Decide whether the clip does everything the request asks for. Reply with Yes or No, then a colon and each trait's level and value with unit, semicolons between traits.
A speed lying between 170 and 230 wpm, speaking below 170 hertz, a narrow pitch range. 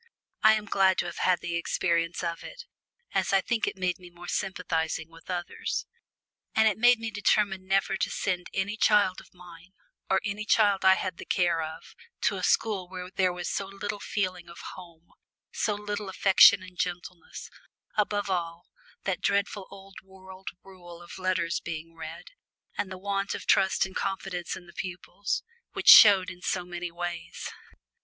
No: average, 180 wpm; medium, 185 Hz; narrow, 2.2 semitones